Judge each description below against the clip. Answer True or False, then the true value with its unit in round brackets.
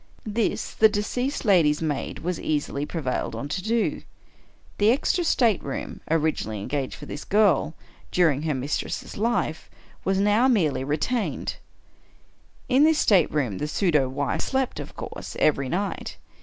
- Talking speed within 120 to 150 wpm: True (145 wpm)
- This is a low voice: False (175 Hz)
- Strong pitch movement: True (7.0 semitones)